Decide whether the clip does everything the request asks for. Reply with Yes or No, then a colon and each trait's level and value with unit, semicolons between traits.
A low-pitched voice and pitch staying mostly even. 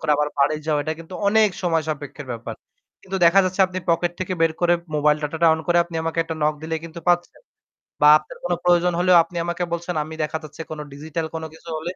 No: medium, 165 Hz; narrow, 2.2 semitones